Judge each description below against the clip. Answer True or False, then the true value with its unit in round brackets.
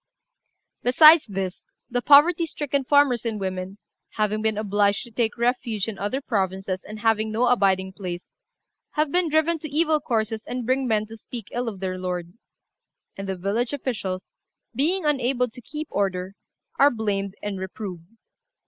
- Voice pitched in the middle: False (220 Hz)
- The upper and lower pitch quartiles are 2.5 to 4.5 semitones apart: False (5.2 semitones)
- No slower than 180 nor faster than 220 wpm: False (160 wpm)